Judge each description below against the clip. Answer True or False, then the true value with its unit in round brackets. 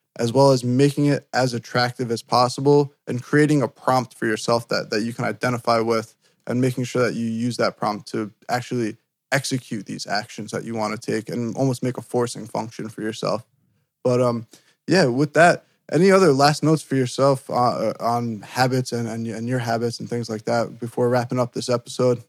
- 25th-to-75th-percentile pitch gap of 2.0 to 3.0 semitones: True (2.5 semitones)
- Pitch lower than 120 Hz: False (125 Hz)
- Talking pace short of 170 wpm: False (200 wpm)